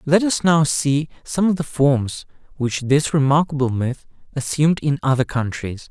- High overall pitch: No, medium, 145 Hz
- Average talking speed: Yes, average, 165 wpm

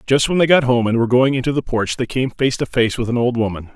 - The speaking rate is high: Yes, fast, 320 wpm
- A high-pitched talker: No, low, 125 Hz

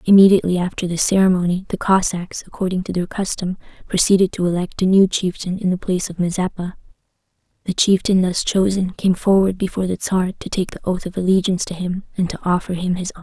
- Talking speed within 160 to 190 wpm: No, average, 200 wpm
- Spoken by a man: No, female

